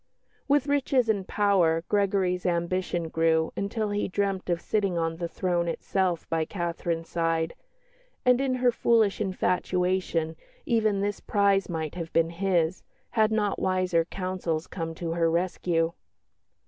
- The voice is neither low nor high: Yes, medium, 180 Hz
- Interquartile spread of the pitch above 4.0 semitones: No, average, 3.4 semitones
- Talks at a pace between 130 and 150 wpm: Yes, average, 140 wpm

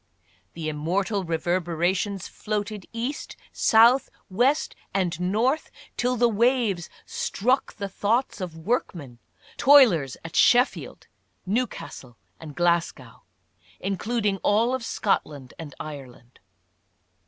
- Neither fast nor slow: No, slow, 105 wpm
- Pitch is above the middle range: Yes, high, 195 Hz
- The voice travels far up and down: Yes, wide, 6.2 semitones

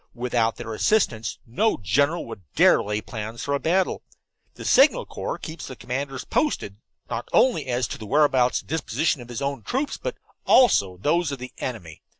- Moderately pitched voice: No, low, 130 Hz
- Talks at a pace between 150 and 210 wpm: Yes, average, 185 wpm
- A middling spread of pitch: No, wide, 6.1 semitones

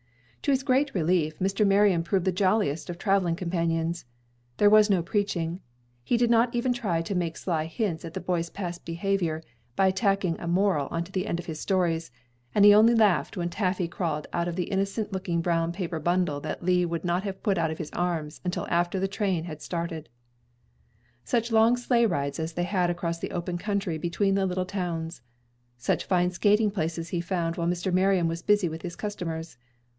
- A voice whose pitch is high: No, medium, 180 Hz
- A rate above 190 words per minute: Yes, average, 200 wpm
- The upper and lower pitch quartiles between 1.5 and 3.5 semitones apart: Yes, average, 2.9 semitones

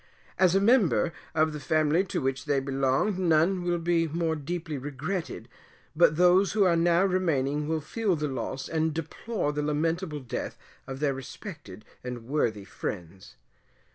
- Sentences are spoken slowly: No, average, 160 wpm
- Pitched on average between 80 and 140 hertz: No, medium, 155 Hz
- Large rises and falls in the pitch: No, average, 4.1 semitones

